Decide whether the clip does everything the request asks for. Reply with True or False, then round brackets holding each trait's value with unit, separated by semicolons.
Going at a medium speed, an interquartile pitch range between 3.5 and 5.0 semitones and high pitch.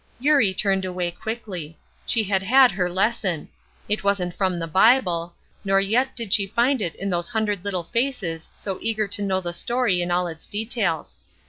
True (185 wpm; 3.9 semitones; 195 Hz)